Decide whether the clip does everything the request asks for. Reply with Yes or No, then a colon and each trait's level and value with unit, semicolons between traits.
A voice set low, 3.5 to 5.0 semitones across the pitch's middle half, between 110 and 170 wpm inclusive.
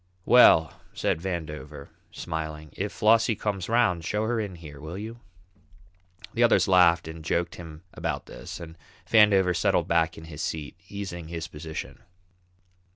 Yes: very low, 85 Hz; average, 4.1 semitones; average, 150 wpm